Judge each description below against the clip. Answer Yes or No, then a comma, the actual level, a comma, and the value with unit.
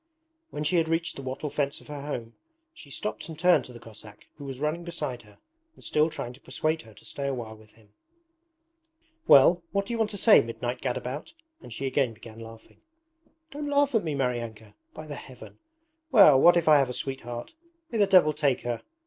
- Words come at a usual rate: No, fast, 215 wpm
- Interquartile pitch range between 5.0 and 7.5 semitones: Yes, wide, 5.6 semitones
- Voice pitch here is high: No, medium, 140 Hz